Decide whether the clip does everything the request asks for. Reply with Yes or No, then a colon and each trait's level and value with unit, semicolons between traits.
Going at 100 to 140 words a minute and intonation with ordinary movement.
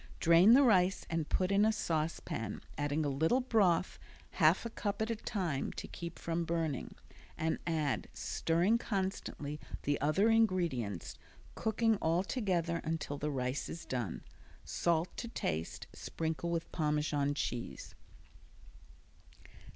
Yes: slow, 135 wpm; average, 4.7 semitones